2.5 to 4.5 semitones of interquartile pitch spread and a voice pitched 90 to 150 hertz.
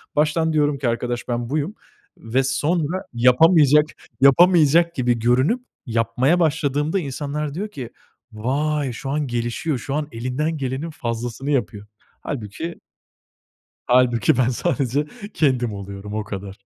Yes: average, 4.2 semitones; low, 135 Hz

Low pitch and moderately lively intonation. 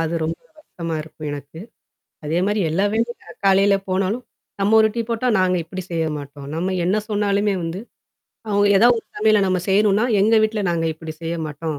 No: high, 190 Hz; average, 4.3 semitones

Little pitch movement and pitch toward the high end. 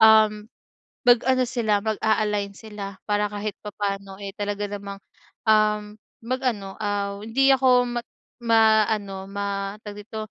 Yes: narrow, 1.6 semitones; high, 210 Hz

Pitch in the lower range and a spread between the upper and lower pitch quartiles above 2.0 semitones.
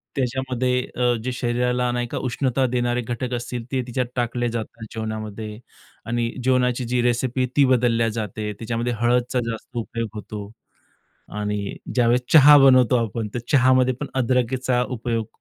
No: low, 120 Hz; narrow, 1.7 semitones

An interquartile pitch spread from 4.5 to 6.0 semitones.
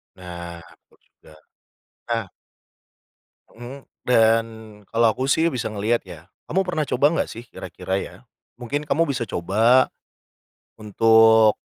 No: average, 3.7 semitones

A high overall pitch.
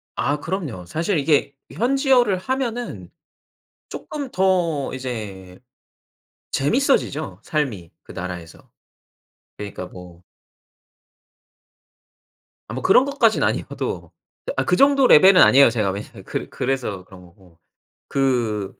No: low, 135 Hz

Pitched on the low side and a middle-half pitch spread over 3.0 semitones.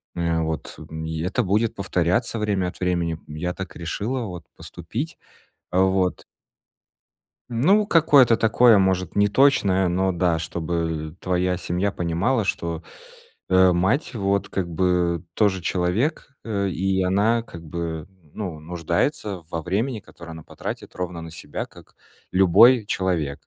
Yes: very low, 90 Hz; average, 3.6 semitones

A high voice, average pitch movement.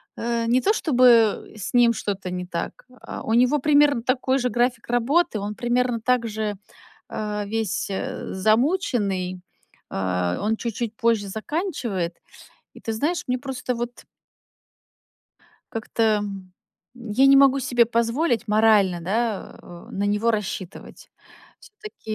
Yes: high, 230 Hz; average, 3.3 semitones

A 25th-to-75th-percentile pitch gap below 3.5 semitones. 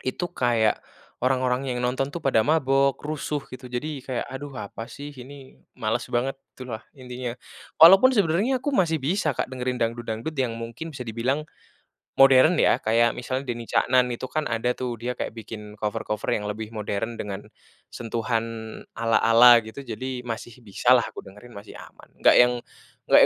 Yes: average, 2.9 semitones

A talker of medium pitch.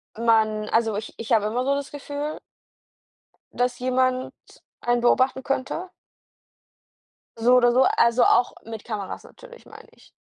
No: high, 245 Hz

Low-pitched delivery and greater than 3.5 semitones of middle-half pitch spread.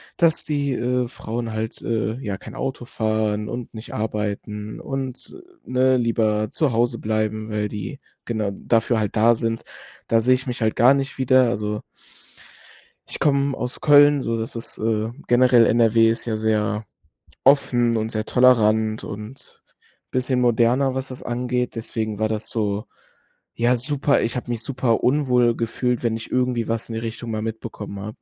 No: low, 115 Hz; narrow, 2.6 semitones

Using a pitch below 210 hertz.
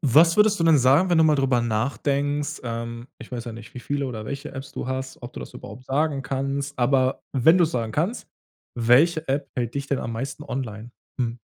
Yes: low, 135 Hz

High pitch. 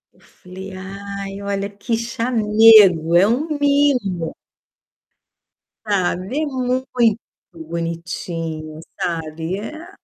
Yes: high, 200 Hz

